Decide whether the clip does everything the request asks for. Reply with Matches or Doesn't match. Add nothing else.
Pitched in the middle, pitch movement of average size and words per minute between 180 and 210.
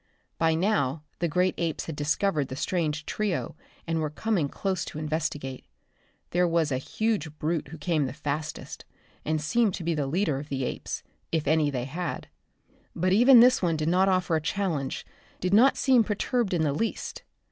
Matches